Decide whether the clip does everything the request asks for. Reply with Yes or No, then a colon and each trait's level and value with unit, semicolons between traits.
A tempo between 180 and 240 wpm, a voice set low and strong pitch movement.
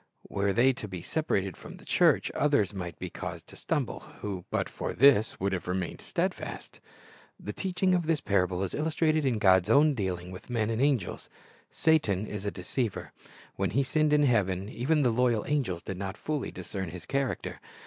Yes: average, 190 wpm; low, 110 Hz; wide, 7.0 semitones